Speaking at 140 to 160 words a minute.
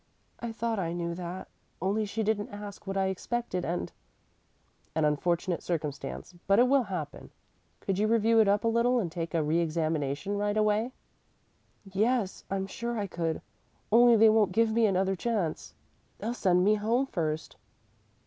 No: average, 170 wpm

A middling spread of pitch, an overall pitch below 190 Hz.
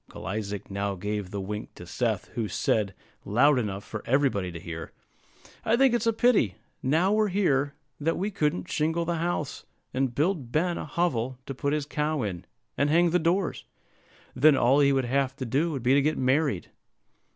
No: wide, 7.2 semitones; medium, 140 Hz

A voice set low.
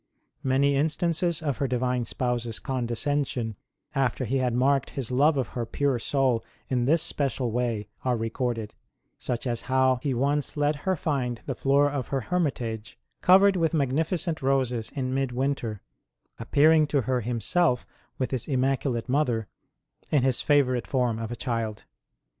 Yes: low, 130 Hz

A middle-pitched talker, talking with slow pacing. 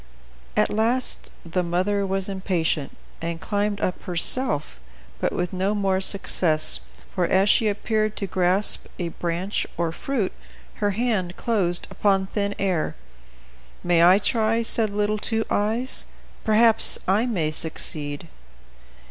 No: high, 195 Hz; slow, 130 wpm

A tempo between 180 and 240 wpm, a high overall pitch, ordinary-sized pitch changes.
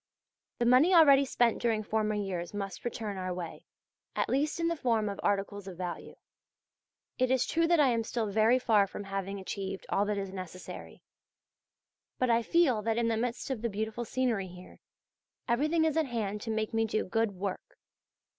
Yes: average, 190 wpm; high, 220 Hz; average, 4.1 semitones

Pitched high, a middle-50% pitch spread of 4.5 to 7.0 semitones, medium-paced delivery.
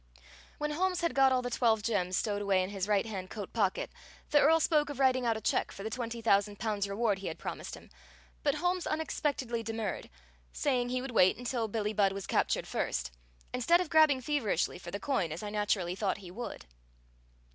No: high, 225 Hz; average, 4.9 semitones; fast, 210 wpm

